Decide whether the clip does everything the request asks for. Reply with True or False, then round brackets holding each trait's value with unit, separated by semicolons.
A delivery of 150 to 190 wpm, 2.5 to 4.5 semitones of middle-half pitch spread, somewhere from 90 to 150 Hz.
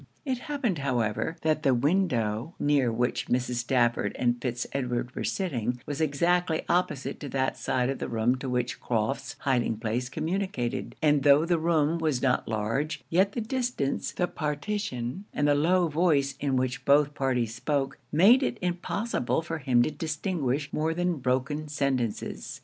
False (165 wpm; 4.9 semitones; 140 Hz)